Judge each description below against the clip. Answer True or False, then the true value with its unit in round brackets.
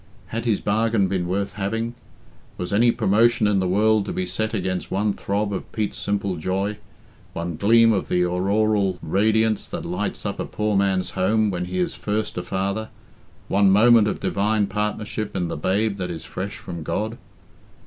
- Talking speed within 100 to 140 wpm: False (180 wpm)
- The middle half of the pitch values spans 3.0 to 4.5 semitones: False (2.6 semitones)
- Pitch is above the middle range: False (100 Hz)